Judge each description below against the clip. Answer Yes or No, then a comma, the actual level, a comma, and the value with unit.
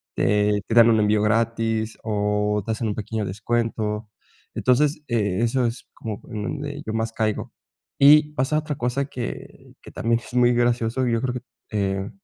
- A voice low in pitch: Yes, low, 115 Hz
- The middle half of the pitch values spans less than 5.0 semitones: Yes, average, 2.7 semitones